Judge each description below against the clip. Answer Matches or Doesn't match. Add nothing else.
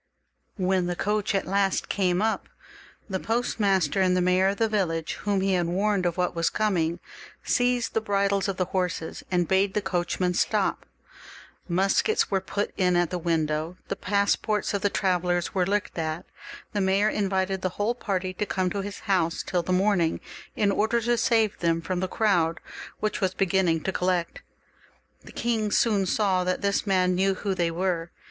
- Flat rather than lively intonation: Matches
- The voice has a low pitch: Doesn't match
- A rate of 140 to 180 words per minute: Doesn't match